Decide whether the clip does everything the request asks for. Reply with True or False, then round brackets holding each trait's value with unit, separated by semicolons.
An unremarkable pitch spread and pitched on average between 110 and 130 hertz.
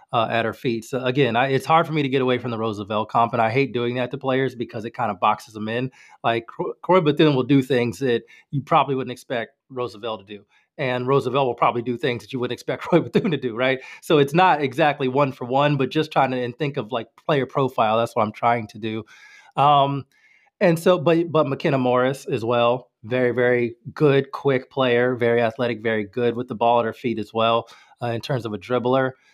True (3.0 semitones; 125 Hz)